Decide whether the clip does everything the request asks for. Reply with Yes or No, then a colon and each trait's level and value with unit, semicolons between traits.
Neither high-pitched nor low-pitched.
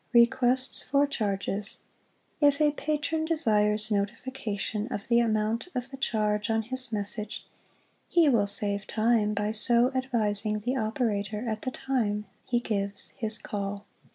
No: high, 220 Hz